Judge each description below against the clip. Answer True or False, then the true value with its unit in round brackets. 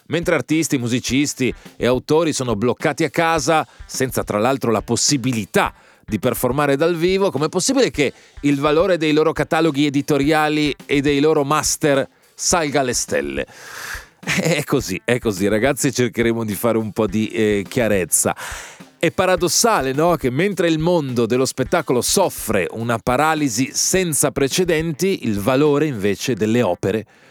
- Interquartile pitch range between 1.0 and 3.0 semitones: False (5.0 semitones)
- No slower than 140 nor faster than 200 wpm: True (145 wpm)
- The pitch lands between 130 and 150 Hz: True (140 Hz)